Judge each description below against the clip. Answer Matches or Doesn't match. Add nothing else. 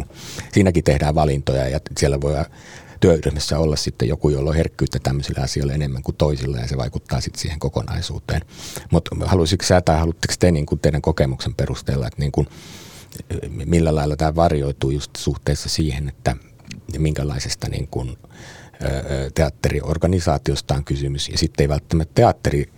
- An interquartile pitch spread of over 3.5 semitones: Doesn't match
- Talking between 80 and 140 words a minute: Doesn't match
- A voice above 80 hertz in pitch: Doesn't match